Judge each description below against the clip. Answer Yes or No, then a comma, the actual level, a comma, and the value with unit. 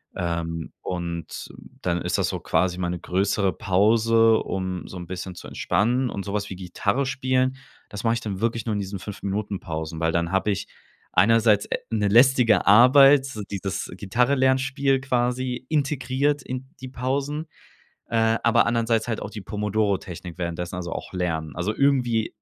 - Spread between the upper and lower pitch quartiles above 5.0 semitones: Yes, wide, 5.4 semitones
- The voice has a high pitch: No, low, 105 Hz